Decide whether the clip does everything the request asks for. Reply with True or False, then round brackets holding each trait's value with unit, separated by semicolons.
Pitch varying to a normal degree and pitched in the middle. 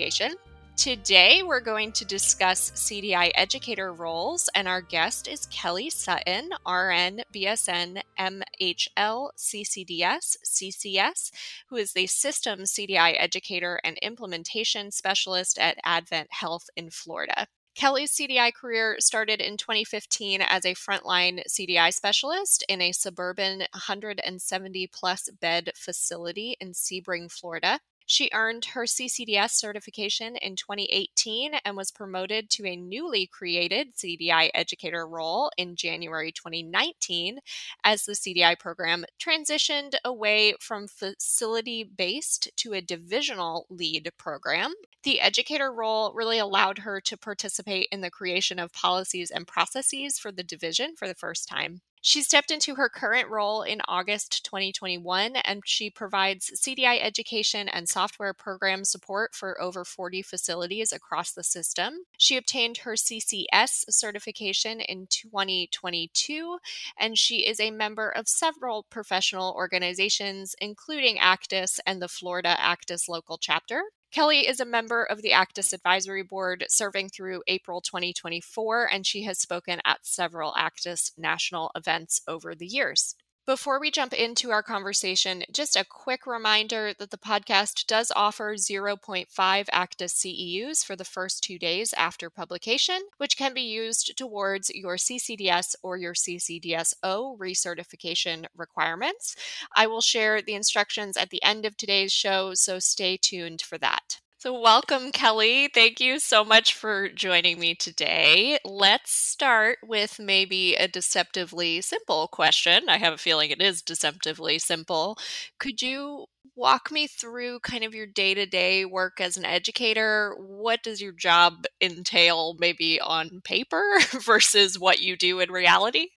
False (3.9 semitones; 195 Hz)